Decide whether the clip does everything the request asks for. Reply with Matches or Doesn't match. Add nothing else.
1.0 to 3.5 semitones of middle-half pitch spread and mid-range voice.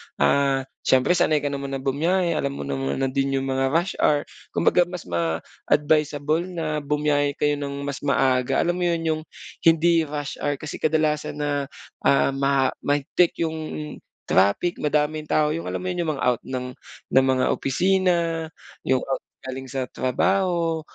Matches